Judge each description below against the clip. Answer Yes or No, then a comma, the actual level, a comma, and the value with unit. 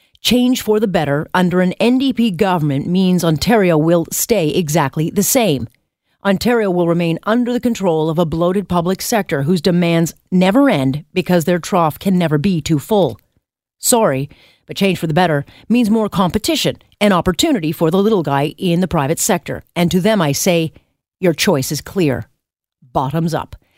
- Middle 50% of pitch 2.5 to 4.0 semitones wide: No, average, 4.5 semitones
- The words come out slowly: No, average, 170 wpm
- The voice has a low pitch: No, medium, 175 Hz